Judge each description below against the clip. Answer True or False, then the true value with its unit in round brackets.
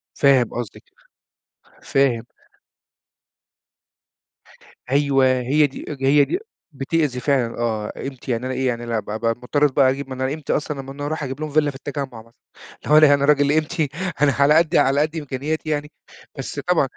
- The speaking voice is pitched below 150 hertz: True (140 Hz)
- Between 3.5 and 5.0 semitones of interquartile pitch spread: False (2.6 semitones)